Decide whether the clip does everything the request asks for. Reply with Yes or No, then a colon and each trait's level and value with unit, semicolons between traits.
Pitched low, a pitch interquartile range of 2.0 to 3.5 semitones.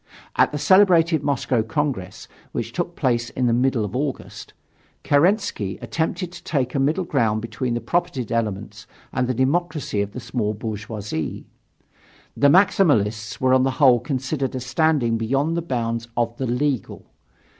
No: low, 130 Hz; average, 4.5 semitones